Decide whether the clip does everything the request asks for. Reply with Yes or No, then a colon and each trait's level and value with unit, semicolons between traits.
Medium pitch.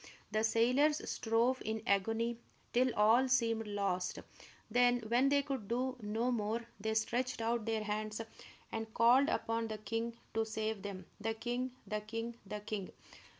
No: high, 225 Hz